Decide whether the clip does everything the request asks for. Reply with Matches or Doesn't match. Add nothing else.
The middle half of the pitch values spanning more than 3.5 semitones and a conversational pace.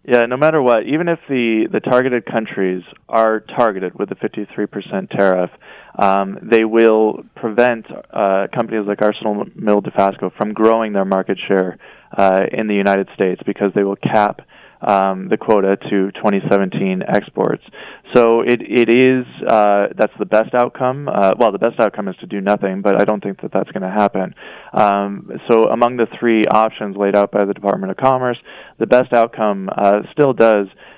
Doesn't match